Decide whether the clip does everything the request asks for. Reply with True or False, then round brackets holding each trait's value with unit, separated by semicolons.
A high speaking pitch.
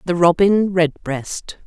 False (175 Hz)